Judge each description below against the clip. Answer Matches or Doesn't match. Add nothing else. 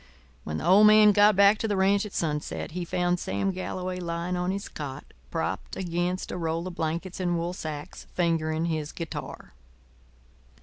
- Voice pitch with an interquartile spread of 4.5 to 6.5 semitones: Doesn't match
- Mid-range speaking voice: Matches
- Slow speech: Doesn't match